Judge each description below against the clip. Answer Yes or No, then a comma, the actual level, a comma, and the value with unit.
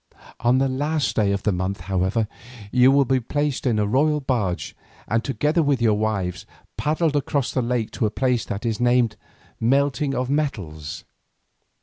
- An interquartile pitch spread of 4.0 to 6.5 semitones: Yes, average, 4.9 semitones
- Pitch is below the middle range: Yes, low, 125 Hz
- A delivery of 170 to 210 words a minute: Yes, average, 175 wpm